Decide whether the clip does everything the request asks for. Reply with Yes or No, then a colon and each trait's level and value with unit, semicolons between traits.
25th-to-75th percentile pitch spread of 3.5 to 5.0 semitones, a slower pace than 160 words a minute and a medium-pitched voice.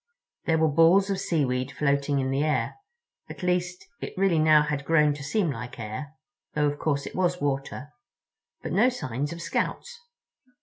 No: average, 4.3 semitones; average, 165 wpm; medium, 150 Hz